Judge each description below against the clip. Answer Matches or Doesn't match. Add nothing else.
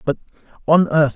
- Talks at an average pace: Matches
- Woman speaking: Doesn't match